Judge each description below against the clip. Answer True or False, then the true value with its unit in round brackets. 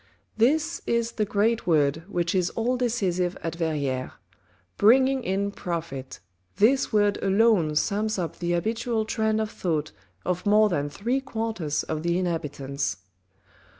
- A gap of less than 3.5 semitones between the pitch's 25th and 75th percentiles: False (5.4 semitones)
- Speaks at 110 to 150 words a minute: True (140 wpm)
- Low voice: False (195 Hz)